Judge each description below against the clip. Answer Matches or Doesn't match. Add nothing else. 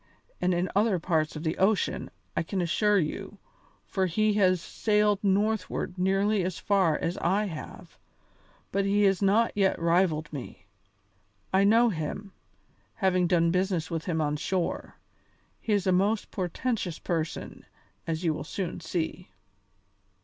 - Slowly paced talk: Doesn't match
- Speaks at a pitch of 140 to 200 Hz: Matches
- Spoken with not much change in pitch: Doesn't match